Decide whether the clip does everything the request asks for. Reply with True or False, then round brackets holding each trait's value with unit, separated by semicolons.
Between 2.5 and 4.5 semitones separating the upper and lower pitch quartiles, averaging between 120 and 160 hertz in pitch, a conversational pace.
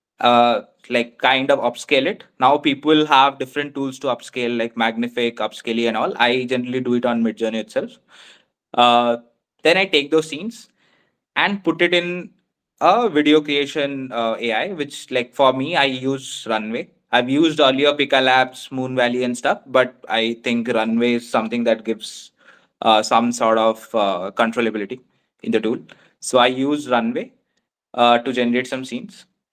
True (2.9 semitones; 125 Hz; 170 wpm)